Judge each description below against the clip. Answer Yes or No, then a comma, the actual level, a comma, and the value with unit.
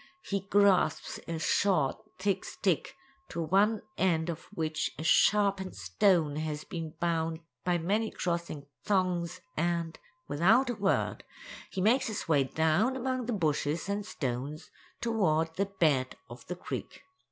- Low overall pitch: No, medium, 175 Hz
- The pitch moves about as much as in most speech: Yes, average, 4.2 semitones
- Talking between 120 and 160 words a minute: Yes, average, 140 wpm